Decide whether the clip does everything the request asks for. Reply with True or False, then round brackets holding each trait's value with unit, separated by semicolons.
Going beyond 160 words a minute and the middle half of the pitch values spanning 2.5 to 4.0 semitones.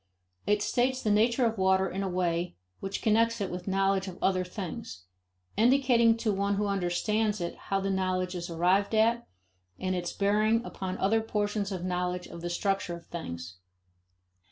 True (175 wpm; 3.1 semitones)